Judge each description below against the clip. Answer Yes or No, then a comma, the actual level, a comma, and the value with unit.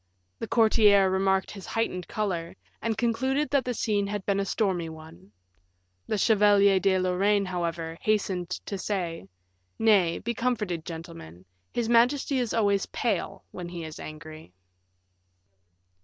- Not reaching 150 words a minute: Yes, average, 140 wpm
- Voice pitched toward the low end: No, high, 195 Hz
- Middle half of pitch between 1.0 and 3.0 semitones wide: No, average, 4.1 semitones